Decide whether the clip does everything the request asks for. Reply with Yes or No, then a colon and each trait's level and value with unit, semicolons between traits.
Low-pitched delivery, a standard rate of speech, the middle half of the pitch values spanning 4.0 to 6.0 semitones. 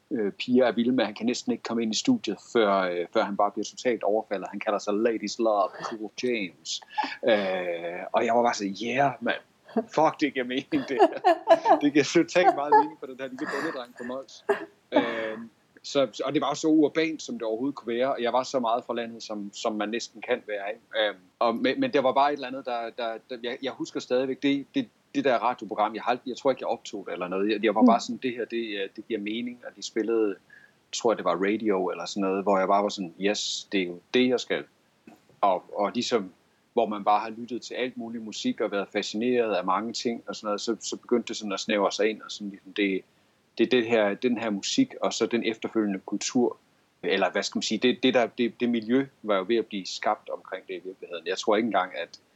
No: low, 115 Hz; fast, 245 wpm; average, 4.3 semitones